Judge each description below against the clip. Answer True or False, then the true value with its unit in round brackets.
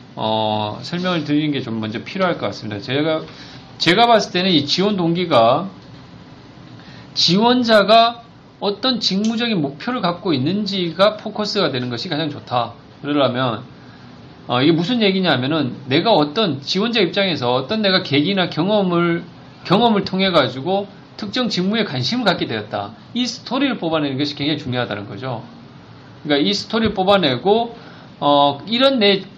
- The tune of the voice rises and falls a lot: True (6.8 semitones)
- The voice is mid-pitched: True (170 Hz)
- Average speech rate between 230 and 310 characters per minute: False (325 characters per minute)